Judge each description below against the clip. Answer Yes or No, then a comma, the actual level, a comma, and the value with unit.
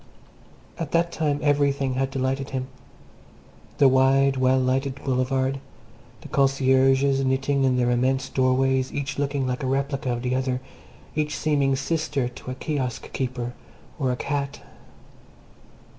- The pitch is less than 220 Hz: Yes, low, 135 Hz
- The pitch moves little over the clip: Yes, narrow, 1.3 semitones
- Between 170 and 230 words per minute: No, average, 140 wpm